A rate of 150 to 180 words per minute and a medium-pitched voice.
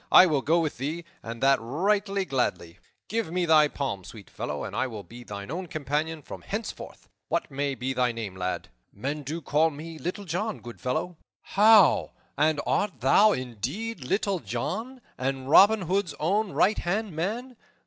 Yes: average, 175 wpm; medium, 155 Hz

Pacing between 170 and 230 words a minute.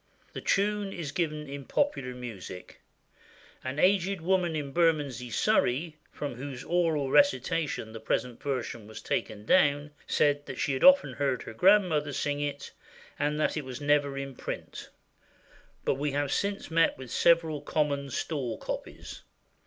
No: average, 155 wpm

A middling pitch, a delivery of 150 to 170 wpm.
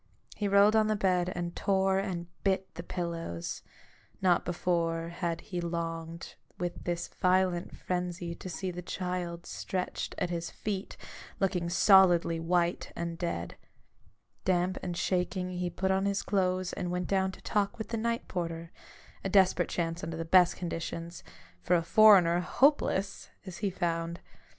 Yes: medium, 180 Hz; average, 160 wpm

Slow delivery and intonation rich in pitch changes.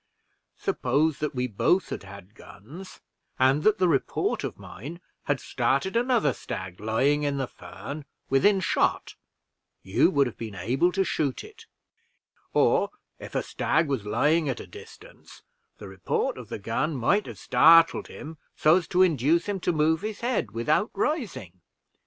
No: average, 160 wpm; wide, 6.4 semitones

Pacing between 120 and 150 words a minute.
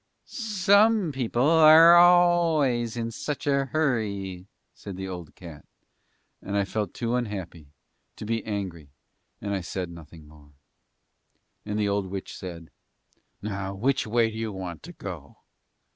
Yes: average, 145 wpm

